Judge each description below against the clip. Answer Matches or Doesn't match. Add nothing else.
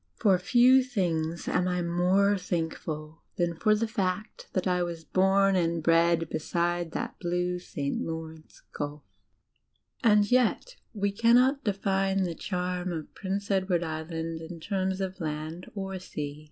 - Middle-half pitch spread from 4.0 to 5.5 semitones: Doesn't match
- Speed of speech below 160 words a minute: Matches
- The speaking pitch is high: Doesn't match